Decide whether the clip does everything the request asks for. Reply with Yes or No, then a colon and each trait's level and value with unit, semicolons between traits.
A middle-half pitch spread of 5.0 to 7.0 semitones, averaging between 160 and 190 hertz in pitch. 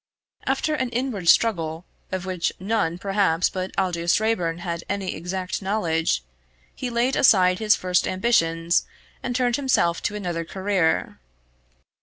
No: average, 4.4 semitones; medium, 185 Hz